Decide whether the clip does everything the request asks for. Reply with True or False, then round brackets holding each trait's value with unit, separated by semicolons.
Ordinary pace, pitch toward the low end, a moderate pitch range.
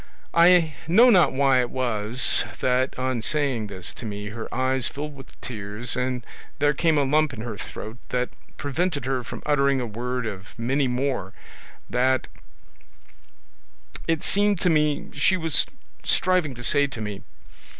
True (160 wpm; 130 Hz; 3.9 semitones)